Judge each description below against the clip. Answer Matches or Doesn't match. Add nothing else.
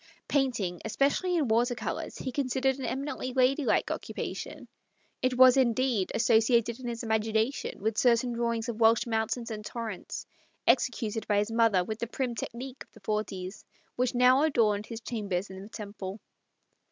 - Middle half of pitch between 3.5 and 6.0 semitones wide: Doesn't match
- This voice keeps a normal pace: Matches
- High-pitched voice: Matches